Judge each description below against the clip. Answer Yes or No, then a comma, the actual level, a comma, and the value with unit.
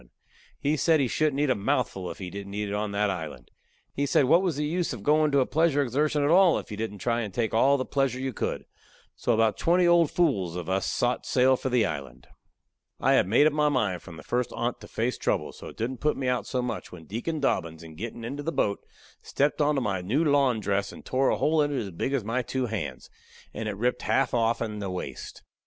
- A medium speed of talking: No, fast, 250 wpm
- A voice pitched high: No, low, 125 Hz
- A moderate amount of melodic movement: No, wide, 5.9 semitones